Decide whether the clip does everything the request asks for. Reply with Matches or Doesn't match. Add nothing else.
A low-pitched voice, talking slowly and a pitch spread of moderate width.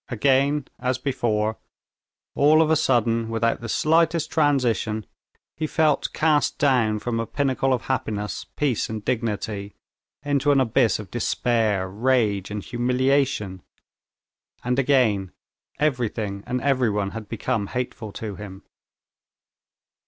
Matches